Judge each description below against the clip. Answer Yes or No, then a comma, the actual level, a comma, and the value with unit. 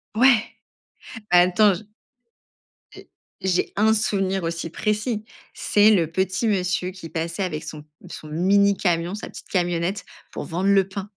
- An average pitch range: Yes, average, 3.0 semitones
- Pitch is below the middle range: No, high, 190 Hz